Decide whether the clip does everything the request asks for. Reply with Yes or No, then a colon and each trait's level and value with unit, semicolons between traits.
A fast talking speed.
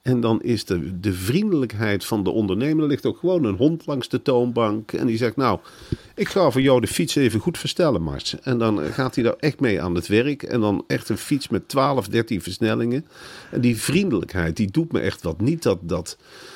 Yes: fast, 225 wpm